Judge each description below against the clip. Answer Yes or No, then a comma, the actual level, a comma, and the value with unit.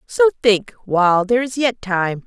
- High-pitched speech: Yes, high, 210 Hz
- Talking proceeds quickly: No, average, 185 wpm